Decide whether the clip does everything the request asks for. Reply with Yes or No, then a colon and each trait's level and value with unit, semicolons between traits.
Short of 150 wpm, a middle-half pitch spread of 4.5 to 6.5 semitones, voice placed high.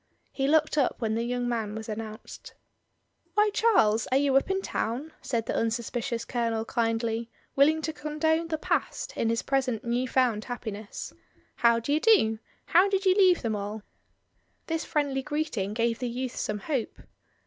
No: average, 170 wpm; average, 5.2 semitones; high, 245 Hz